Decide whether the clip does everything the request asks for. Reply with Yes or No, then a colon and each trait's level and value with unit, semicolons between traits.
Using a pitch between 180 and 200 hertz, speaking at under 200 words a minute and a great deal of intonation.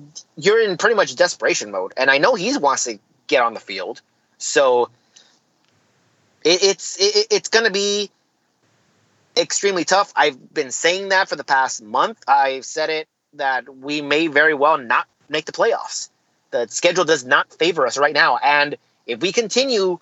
Yes: medium, 185 Hz; average, 170 wpm; wide, 7.1 semitones